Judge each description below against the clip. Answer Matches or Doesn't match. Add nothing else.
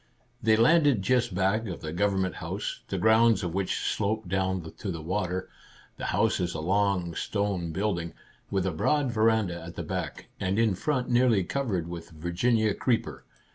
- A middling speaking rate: Matches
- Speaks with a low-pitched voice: Matches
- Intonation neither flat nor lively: Matches